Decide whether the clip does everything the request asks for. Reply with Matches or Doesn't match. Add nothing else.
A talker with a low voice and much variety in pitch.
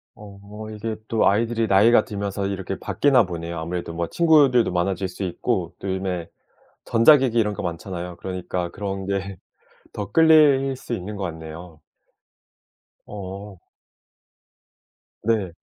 Doesn't match